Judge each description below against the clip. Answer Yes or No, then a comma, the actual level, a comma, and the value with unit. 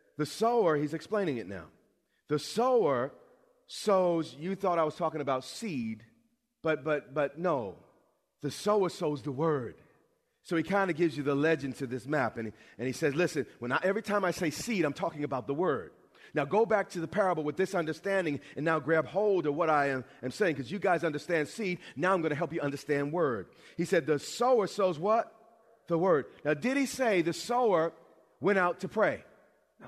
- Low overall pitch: No, medium, 165 Hz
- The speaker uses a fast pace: Yes, fast, 210 wpm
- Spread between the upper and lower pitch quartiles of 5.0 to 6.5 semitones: Yes, wide, 5.4 semitones